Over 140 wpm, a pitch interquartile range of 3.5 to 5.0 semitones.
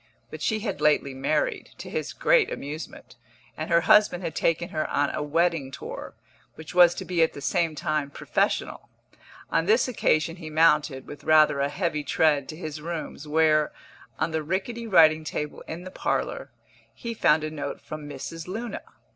No: average, 180 wpm; average, 2.7 semitones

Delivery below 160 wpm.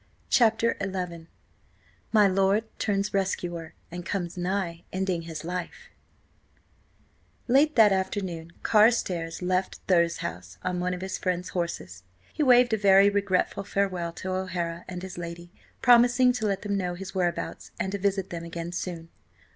Yes: average, 150 wpm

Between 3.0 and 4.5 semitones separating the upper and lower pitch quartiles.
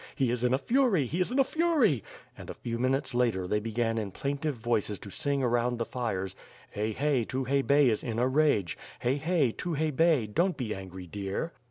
No: average, 5.0 semitones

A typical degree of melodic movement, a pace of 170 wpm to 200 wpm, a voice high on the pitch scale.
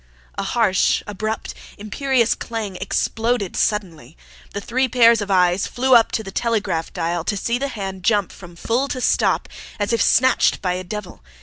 Yes: average, 3.9 semitones; average, 175 wpm; high, 210 Hz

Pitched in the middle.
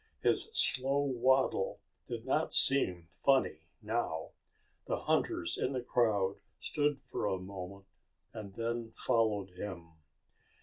No: low, 115 Hz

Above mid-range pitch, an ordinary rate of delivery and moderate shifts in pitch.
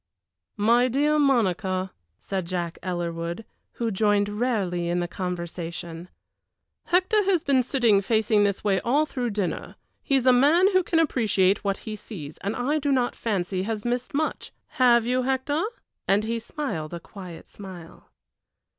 No: high, 215 Hz; average, 155 wpm; wide, 5.8 semitones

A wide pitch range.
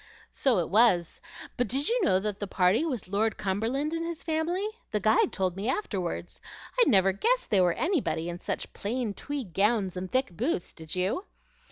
Yes: wide, 7.7 semitones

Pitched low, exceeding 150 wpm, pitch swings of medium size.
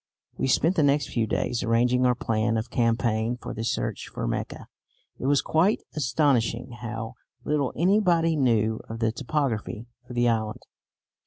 Yes: low, 120 Hz; average, 160 wpm; average, 4.0 semitones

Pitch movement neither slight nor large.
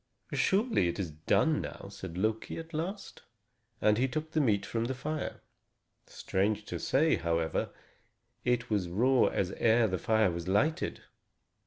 No: wide, 7.9 semitones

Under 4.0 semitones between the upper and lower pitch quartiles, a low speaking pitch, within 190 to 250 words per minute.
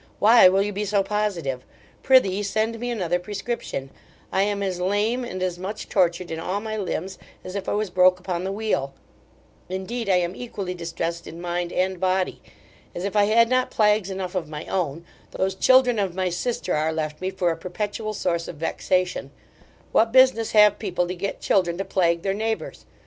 No: average, 3.0 semitones; high, 190 Hz; average, 195 wpm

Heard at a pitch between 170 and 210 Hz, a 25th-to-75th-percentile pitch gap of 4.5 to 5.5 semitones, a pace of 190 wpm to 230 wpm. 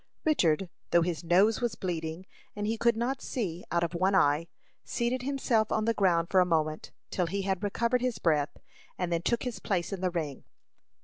Yes: high, 190 Hz; average, 5.2 semitones; average, 200 wpm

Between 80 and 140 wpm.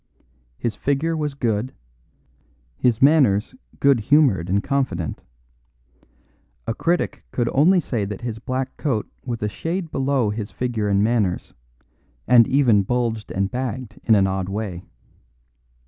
Yes: slow, 135 wpm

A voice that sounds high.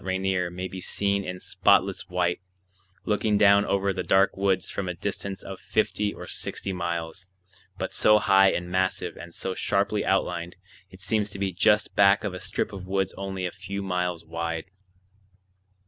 No: very low, 95 Hz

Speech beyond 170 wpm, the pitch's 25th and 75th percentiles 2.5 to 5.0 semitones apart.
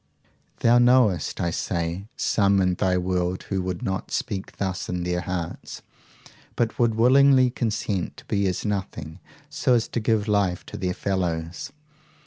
No: average, 150 wpm; average, 3.7 semitones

